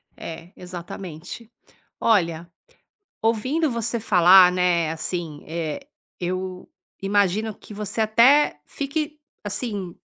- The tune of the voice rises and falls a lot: No, average, 4.5 semitones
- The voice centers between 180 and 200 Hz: Yes, high, 190 Hz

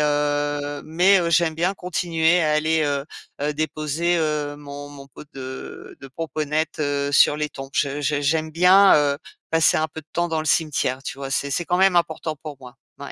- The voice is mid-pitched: Yes, medium, 155 Hz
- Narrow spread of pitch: Yes, narrow, 2.2 semitones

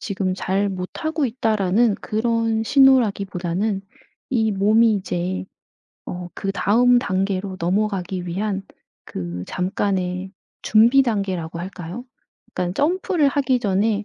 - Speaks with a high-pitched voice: Yes, high, 200 Hz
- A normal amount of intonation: Yes, average, 3.6 semitones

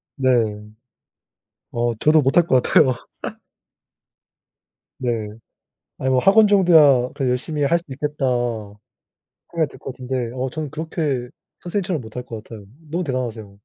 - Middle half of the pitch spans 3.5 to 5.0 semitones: Yes, average, 4.2 semitones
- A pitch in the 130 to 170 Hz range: Yes, low, 135 Hz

